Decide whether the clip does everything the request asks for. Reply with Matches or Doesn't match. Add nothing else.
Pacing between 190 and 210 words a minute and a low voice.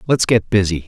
Matches